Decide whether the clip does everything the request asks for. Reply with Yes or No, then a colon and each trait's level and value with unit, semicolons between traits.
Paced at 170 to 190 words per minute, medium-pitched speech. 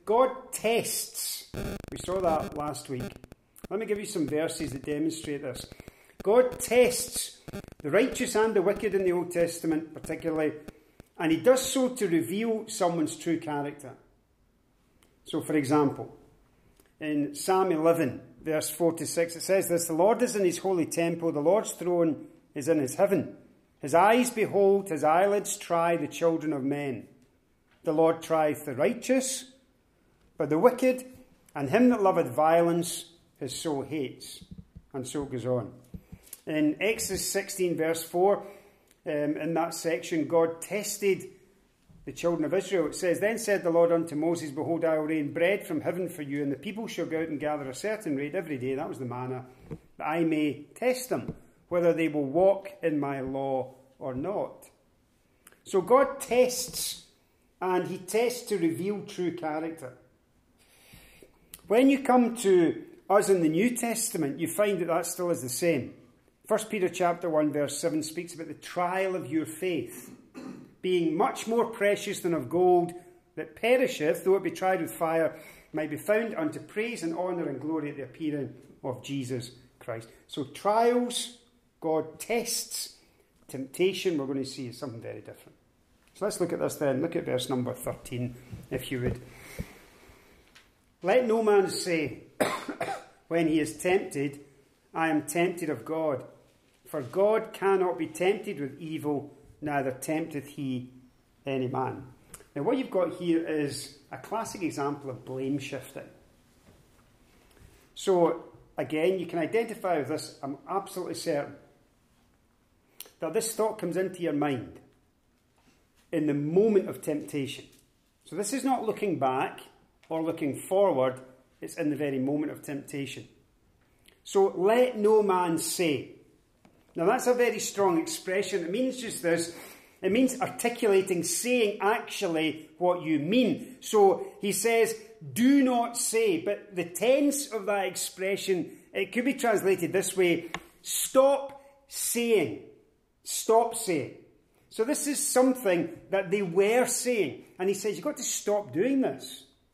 No: average, 155 wpm; medium, 170 Hz